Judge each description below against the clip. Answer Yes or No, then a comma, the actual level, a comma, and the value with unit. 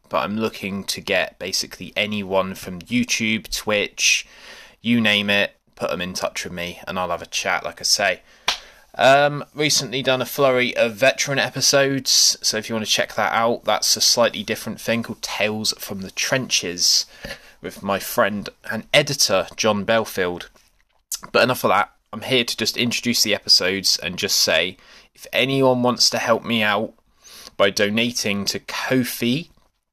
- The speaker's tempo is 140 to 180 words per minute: Yes, average, 170 wpm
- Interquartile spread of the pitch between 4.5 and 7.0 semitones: No, average, 3.9 semitones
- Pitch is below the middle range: Yes, low, 115 Hz